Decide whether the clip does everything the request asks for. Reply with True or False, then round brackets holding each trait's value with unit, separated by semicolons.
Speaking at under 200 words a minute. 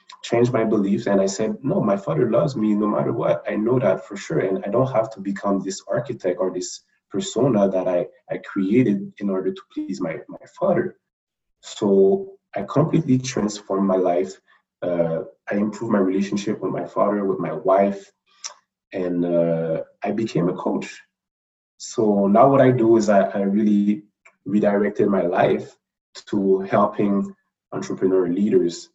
True (165 wpm)